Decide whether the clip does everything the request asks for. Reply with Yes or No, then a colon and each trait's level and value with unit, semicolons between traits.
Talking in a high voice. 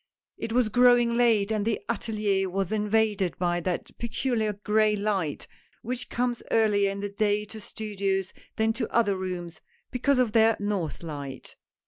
Yes: high, 210 Hz